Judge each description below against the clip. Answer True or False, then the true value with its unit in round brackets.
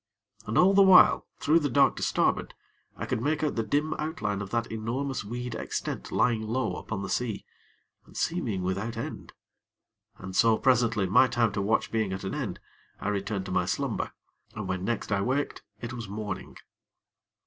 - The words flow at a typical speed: True (185 wpm)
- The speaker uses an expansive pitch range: False (4.2 semitones)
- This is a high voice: False (115 Hz)